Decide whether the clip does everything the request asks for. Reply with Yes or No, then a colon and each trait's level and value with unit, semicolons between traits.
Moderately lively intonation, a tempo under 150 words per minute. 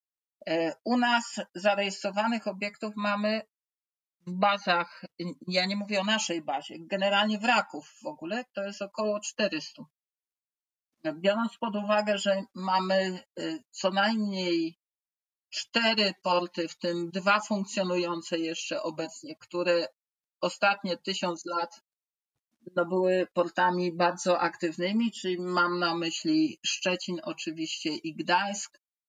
Yes: average, 3.2 semitones; slow, 110 wpm